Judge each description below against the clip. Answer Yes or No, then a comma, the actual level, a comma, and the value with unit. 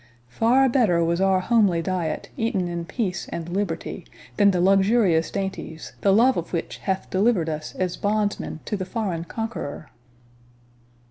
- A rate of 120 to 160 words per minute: Yes, average, 150 wpm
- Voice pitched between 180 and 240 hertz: Yes, high, 190 Hz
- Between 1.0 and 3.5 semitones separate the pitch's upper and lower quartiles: No, average, 3.9 semitones